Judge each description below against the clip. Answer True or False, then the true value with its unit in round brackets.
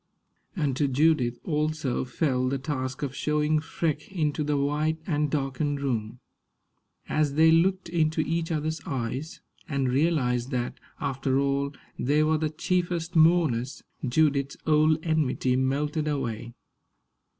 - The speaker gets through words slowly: True (130 wpm)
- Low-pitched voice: False (150 Hz)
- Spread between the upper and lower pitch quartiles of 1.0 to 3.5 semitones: True (2.9 semitones)